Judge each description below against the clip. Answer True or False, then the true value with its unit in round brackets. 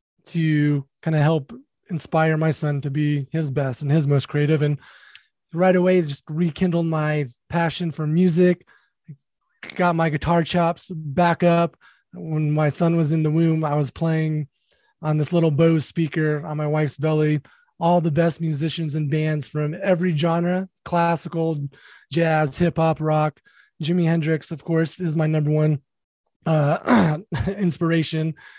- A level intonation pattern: True (2.0 semitones)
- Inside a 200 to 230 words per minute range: False (155 wpm)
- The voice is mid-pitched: True (160 Hz)